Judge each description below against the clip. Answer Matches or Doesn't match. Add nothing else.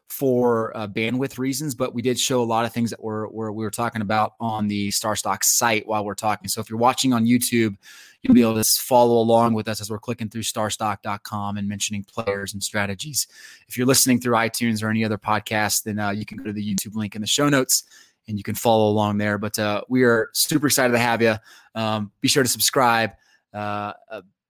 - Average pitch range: Doesn't match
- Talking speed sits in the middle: Doesn't match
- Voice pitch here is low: Matches